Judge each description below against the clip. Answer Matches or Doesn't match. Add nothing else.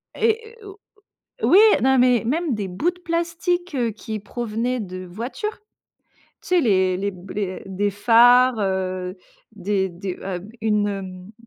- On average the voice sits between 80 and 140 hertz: Doesn't match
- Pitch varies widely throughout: Matches